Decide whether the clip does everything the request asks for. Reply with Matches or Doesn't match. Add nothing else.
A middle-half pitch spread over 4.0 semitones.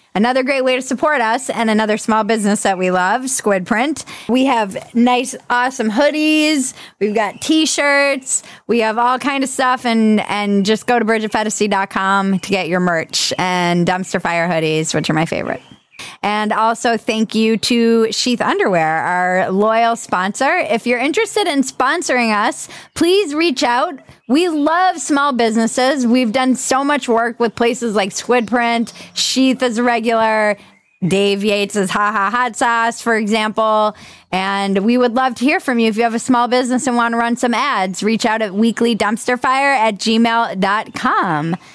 Doesn't match